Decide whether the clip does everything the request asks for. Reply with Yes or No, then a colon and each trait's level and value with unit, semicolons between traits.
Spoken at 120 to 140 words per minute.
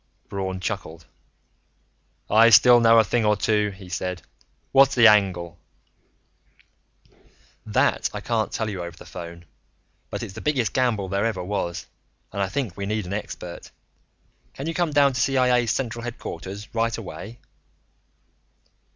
No: average, 150 wpm